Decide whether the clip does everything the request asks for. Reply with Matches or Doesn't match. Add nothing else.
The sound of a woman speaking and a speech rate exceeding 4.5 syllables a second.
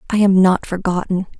Matches